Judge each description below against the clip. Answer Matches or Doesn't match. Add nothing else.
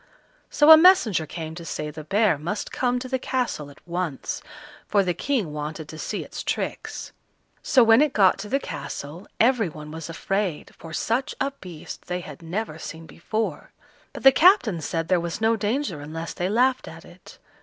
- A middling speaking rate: Matches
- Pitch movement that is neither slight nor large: Doesn't match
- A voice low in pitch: Doesn't match